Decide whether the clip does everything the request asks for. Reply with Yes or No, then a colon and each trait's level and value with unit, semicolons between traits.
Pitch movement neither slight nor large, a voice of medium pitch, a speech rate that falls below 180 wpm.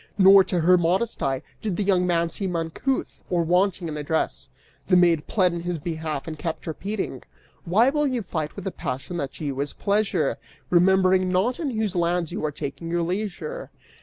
No: average, 3.3 semitones; medium, 180 Hz; average, 195 wpm